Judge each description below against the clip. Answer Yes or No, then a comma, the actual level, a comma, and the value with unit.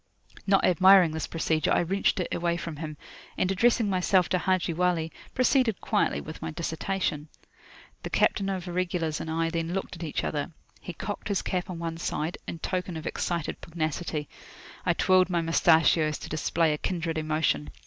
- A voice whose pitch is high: No, medium, 170 Hz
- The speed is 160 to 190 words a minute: Yes, average, 180 wpm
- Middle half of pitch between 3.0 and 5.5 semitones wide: No, narrow, 2.6 semitones